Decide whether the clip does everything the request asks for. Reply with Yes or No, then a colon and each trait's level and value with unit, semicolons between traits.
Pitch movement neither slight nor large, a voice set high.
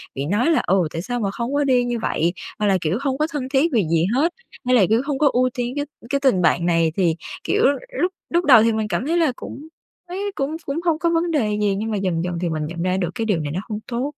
No: wide, 7.6 semitones; high, 235 Hz